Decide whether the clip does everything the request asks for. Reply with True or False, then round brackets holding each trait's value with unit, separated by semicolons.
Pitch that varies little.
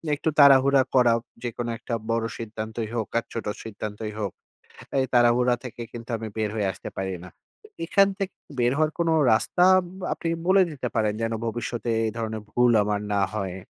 False (3.0 semitones)